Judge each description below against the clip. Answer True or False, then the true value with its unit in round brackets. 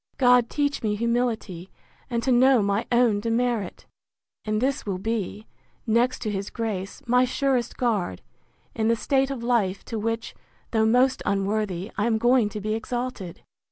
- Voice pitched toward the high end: True (230 Hz)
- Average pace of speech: True (160 wpm)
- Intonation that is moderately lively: True (3.0 semitones)